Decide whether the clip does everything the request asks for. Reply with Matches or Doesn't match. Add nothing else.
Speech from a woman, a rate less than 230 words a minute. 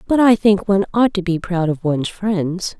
Doesn't match